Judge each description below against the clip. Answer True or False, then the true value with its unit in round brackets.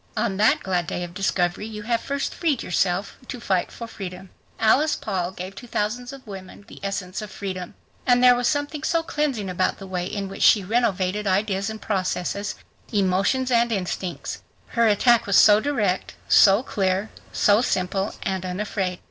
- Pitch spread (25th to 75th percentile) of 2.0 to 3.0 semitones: False (3.8 semitones)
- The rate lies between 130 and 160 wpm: False (175 wpm)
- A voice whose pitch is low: False (200 Hz)